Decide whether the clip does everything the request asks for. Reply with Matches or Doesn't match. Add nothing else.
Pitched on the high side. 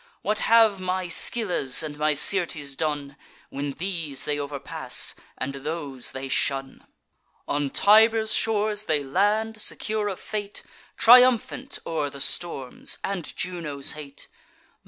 Doesn't match